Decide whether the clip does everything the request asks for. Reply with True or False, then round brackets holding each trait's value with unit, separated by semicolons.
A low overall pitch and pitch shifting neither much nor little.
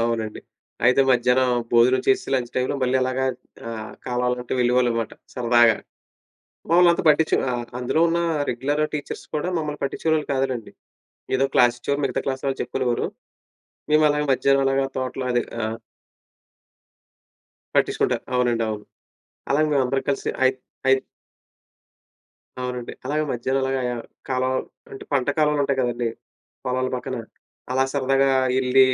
False (130 Hz; 2.0 semitones)